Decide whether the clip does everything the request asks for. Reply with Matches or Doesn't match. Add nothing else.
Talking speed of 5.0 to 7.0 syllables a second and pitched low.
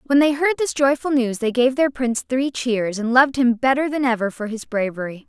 Doesn't match